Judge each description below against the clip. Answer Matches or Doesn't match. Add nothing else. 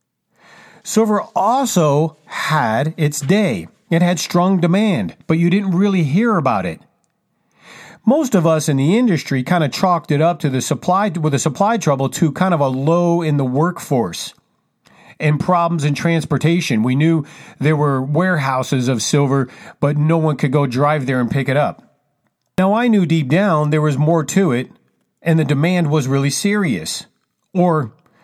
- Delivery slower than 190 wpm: Matches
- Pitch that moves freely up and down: Doesn't match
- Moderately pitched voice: Matches